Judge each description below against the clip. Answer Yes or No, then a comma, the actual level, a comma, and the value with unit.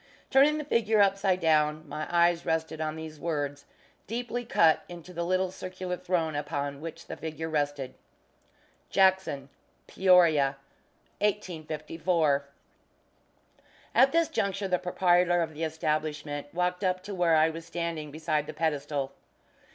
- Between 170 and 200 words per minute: No, slow, 135 wpm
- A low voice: No, medium, 165 Hz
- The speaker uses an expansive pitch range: No, average, 3.2 semitones